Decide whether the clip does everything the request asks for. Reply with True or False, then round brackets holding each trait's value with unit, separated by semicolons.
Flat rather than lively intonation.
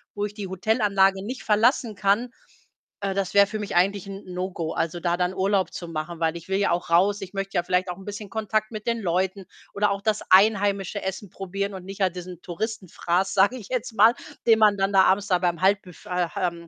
True (2.3 semitones)